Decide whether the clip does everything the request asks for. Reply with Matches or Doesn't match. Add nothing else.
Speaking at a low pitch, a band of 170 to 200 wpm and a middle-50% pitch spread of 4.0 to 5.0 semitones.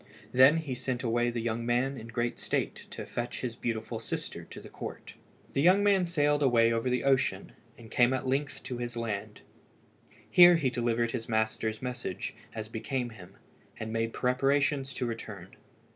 Doesn't match